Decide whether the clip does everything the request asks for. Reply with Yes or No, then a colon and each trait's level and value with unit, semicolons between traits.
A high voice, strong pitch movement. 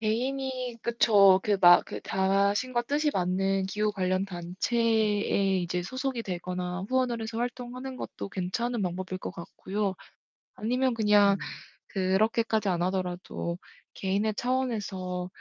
No: high, 205 Hz; average, 4.2 semitones